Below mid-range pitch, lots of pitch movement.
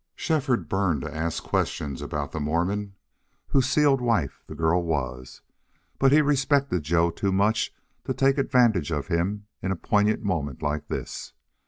Yes: very low, 95 Hz; wide, 8.2 semitones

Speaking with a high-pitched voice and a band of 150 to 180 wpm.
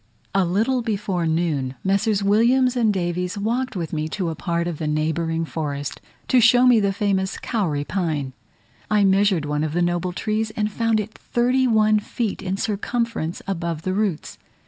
Yes: high, 195 Hz; average, 175 wpm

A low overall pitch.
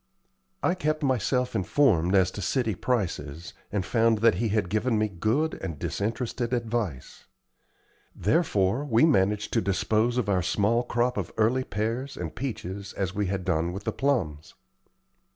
Yes: low, 110 Hz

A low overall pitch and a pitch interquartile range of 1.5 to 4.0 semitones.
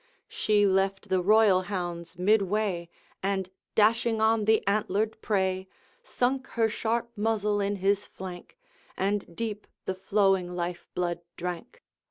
No: high, 200 Hz; average, 2.8 semitones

